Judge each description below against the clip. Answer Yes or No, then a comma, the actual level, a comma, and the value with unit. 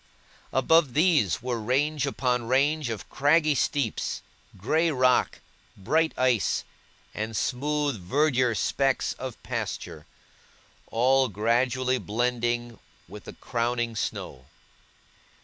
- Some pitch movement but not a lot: Yes, average, 3.6 semitones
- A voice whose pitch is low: Yes, low, 125 Hz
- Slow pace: Yes, slow, 100 wpm